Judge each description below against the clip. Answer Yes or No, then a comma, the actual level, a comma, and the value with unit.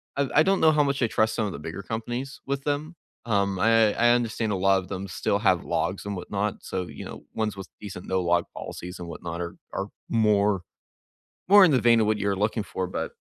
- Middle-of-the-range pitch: No, low, 105 Hz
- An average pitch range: Yes, average, 4.0 semitones